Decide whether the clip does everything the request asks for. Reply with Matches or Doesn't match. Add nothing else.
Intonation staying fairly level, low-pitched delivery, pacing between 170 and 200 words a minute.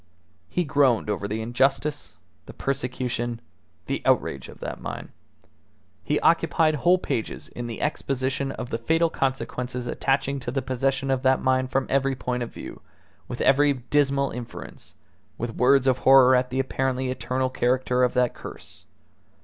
Doesn't match